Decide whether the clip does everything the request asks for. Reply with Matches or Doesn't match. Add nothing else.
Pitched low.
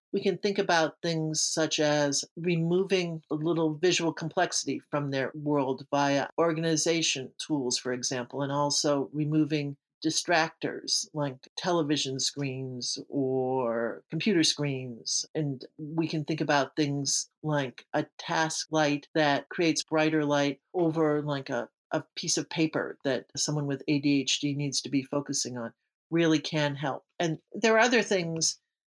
Doesn't match